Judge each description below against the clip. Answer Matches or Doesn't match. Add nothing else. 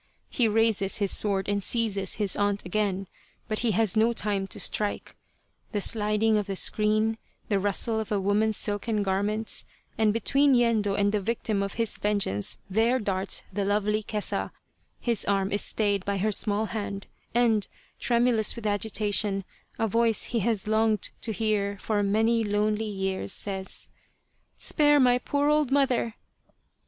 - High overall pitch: Matches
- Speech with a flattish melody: Matches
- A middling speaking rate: Matches